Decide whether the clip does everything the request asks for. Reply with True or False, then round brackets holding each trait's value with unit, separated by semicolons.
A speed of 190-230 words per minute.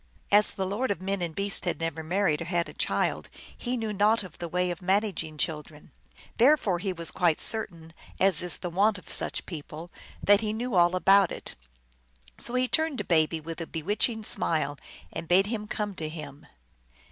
True (200 wpm)